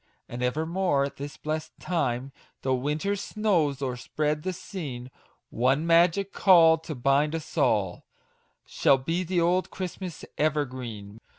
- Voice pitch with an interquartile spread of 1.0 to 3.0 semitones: No, average, 4.8 semitones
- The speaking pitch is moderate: Yes, medium, 150 Hz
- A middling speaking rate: No, slow, 125 wpm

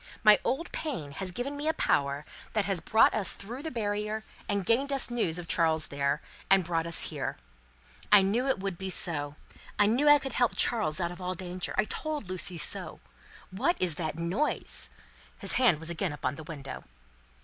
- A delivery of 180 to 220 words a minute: Yes, average, 195 wpm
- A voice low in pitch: No, high, 190 Hz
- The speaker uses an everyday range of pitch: No, wide, 6.3 semitones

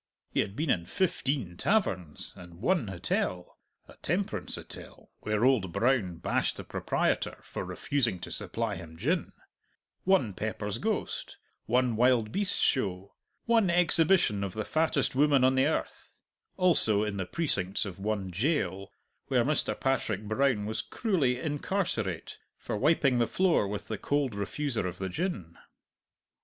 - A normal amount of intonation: No, wide, 7.4 semitones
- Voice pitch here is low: Yes, low, 115 Hz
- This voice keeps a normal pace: Yes, average, 150 wpm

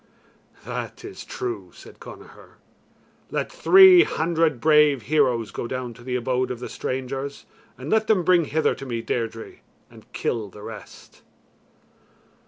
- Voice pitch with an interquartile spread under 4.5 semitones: No, wide, 5.5 semitones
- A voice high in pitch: No, low, 135 Hz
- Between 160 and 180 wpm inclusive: No, average, 145 wpm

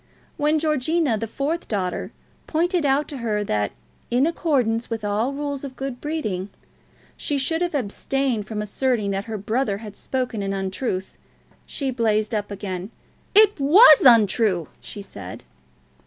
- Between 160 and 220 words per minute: No, average, 150 wpm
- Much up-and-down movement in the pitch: Yes, wide, 5.7 semitones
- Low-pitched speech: No, high, 235 Hz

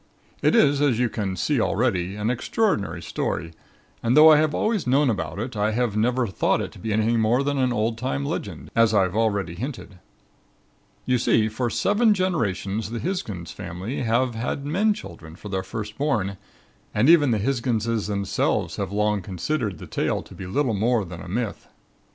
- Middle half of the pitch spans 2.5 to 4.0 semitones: No, average, 4.7 semitones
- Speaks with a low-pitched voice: Yes, low, 115 Hz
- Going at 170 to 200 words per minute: Yes, average, 190 wpm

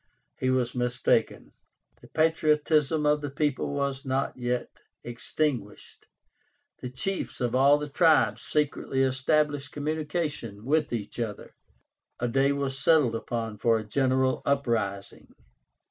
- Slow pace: Yes, slow, 125 wpm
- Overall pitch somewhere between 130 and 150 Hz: Yes, low, 135 Hz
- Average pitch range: Yes, average, 3.6 semitones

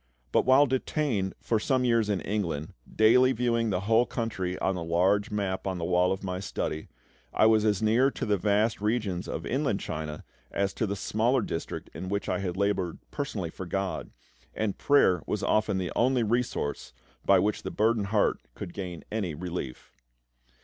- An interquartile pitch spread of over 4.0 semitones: No, average, 3.6 semitones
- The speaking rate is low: No, average, 185 wpm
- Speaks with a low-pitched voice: Yes, low, 100 Hz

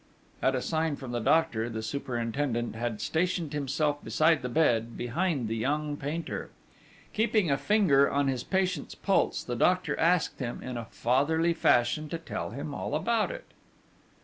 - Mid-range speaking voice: Yes, medium, 145 Hz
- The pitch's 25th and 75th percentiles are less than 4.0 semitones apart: No, average, 5.2 semitones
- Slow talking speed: No, average, 165 wpm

